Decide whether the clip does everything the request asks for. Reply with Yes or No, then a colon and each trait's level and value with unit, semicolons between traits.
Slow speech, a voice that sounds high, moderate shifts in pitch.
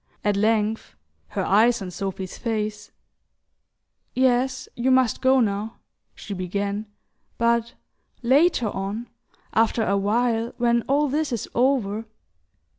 Yes: slow, 115 wpm; high, 225 Hz; average, 3.3 semitones